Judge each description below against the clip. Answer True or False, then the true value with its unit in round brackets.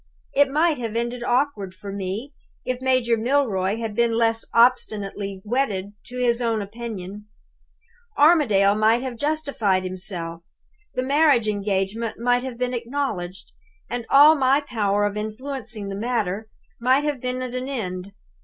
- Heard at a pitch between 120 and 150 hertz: False (230 Hz)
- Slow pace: False (145 wpm)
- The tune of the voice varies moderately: True (4.1 semitones)